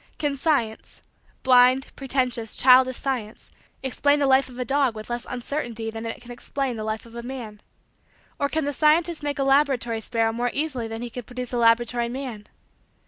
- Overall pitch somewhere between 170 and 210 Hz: No, very high, 250 Hz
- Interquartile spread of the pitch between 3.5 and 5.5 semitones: No, average, 3.0 semitones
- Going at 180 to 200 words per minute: Yes, average, 190 wpm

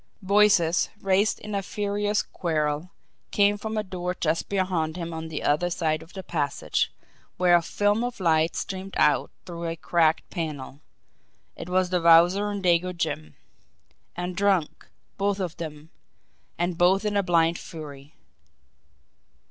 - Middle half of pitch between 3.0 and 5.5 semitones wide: Yes, average, 3.3 semitones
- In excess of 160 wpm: No, average, 150 wpm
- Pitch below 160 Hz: No, medium, 175 Hz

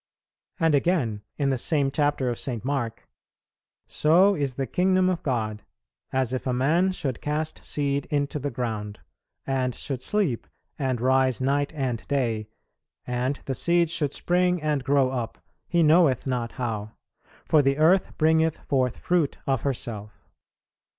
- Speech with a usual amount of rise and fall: Yes, average, 3.8 semitones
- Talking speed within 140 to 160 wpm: Yes, average, 150 wpm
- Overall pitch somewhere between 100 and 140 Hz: Yes, low, 135 Hz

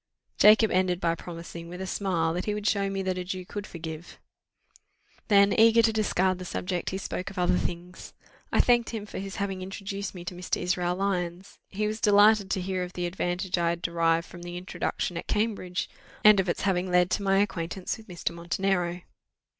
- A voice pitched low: No, medium, 185 Hz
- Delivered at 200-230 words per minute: Yes, fast, 205 wpm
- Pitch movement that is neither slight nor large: No, narrow, 2.2 semitones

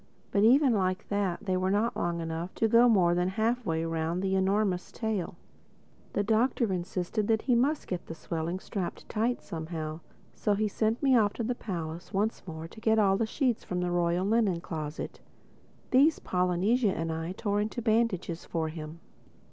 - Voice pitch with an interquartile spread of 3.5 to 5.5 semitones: Yes, average, 4.4 semitones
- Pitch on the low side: No, high, 190 Hz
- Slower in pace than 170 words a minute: No, average, 180 wpm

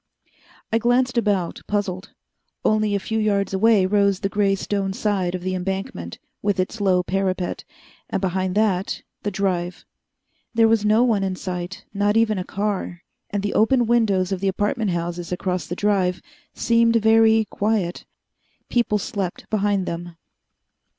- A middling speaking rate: Yes, average, 155 wpm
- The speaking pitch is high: Yes, high, 200 Hz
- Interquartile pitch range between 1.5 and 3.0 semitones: Yes, average, 2.7 semitones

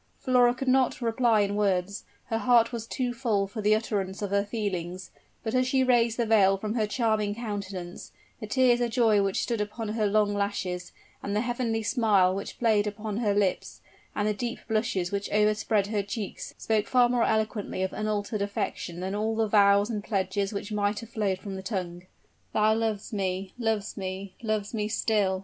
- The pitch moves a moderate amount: No, narrow, 2.2 semitones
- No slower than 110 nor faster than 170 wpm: No, average, 195 wpm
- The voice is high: Yes, high, 210 Hz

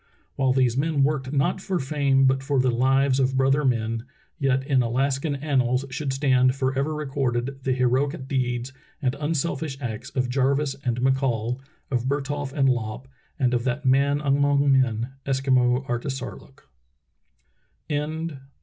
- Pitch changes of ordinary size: No, narrow, 1.6 semitones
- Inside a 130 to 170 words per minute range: Yes, average, 145 wpm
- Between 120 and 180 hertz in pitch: Yes, low, 135 Hz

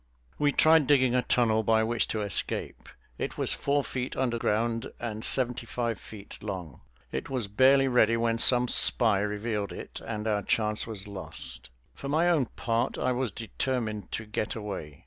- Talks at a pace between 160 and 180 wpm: Yes, average, 175 wpm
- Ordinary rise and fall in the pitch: Yes, average, 3.2 semitones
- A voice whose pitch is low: Yes, low, 115 Hz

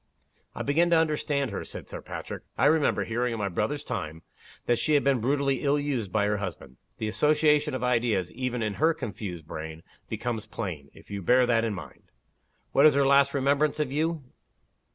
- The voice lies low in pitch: Yes, low, 125 Hz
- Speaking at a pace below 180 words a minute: No, average, 200 wpm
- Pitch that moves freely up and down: Yes, wide, 5.7 semitones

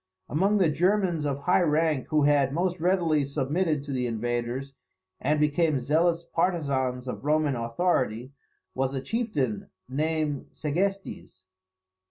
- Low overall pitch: No, medium, 150 Hz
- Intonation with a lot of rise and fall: No, average, 4.2 semitones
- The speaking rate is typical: No, slow, 130 wpm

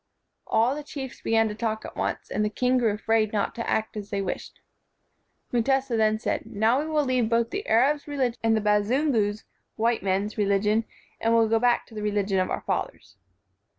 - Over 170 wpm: Yes, average, 200 wpm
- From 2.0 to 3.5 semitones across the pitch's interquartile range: Yes, average, 2.9 semitones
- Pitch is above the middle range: Yes, high, 225 Hz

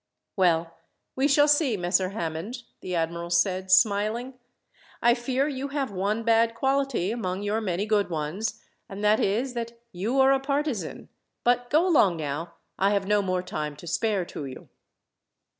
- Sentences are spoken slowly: No, average, 165 wpm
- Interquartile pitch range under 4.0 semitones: No, average, 5.2 semitones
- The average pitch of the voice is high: Yes, high, 210 Hz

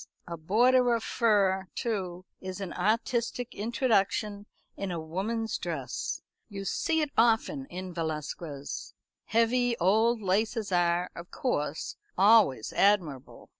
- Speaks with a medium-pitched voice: No, high, 200 Hz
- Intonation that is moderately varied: Yes, average, 4.5 semitones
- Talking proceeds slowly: Yes, slow, 120 wpm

